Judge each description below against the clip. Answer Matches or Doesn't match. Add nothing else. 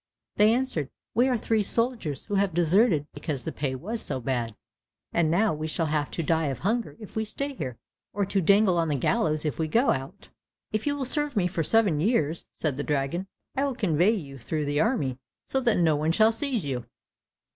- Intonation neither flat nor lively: Doesn't match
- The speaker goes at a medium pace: Doesn't match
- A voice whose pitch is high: Doesn't match